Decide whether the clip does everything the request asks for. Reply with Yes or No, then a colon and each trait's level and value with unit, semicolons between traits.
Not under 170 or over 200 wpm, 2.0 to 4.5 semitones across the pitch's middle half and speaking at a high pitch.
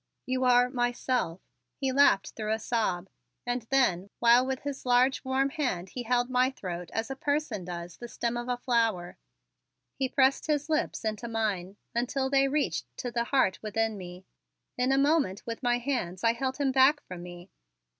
Yes: average, 185 wpm; average, 4.0 semitones; high, 245 Hz